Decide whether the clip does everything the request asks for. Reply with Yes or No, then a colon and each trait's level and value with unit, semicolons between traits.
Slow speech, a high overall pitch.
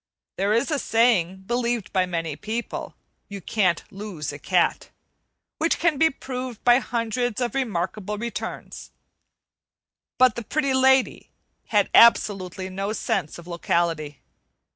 Yes: slow, 130 wpm; high, 215 Hz